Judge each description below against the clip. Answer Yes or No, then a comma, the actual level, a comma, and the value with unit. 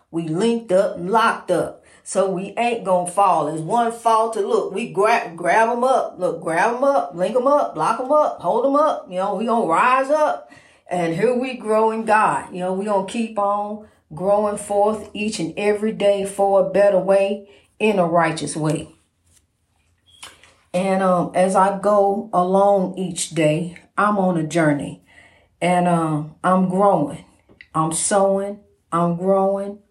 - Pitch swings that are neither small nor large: Yes, average, 3.7 semitones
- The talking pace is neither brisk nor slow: Yes, average, 170 wpm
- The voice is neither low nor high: No, high, 195 Hz